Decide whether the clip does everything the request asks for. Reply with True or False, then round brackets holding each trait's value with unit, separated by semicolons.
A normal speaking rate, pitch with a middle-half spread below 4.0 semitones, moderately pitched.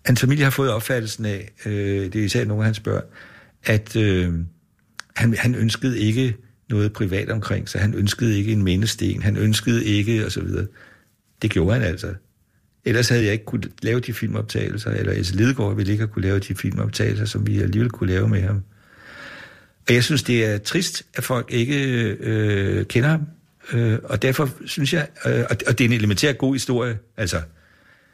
False (190 wpm; 2.9 semitones; 110 Hz)